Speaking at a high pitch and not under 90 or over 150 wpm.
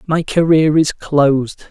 No: medium, 150 Hz; average, 140 wpm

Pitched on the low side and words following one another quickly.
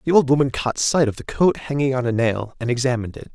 Yes: low, 130 Hz; fast, 270 wpm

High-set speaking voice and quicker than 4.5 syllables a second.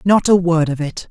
No: medium, 170 Hz; 5.0 syllables/s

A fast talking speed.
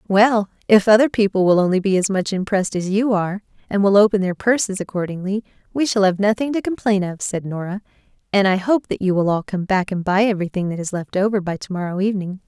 Yes: fast, 230 wpm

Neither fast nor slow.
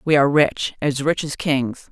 No: fast, 220 wpm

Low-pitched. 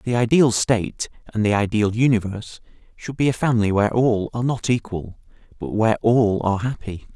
Yes: low, 110 Hz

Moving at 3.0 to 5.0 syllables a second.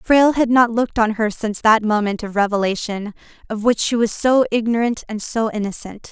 No: 5.6 syllables/s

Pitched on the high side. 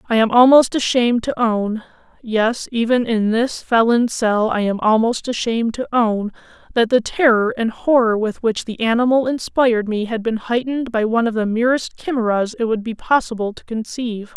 Yes: high, 230 Hz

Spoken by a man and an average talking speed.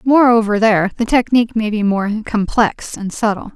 No: female; average, 170 wpm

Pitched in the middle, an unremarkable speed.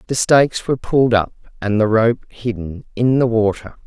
No: low, 115 Hz; average, 185 wpm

